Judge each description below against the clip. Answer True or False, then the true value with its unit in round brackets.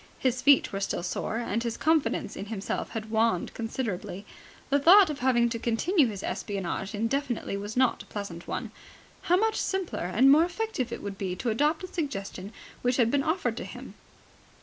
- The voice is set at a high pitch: True (235 Hz)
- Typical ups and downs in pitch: False (6.0 semitones)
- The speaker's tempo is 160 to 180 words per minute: False (190 wpm)